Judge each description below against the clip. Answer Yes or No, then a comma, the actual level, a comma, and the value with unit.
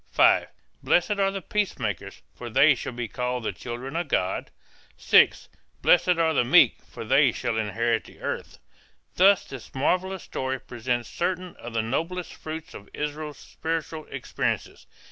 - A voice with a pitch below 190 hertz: Yes, low, 135 Hz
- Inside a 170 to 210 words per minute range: No, average, 155 wpm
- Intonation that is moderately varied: No, wide, 6.3 semitones